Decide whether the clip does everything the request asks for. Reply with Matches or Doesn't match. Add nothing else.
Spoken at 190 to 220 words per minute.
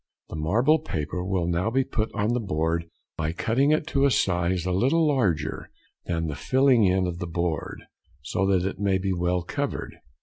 Matches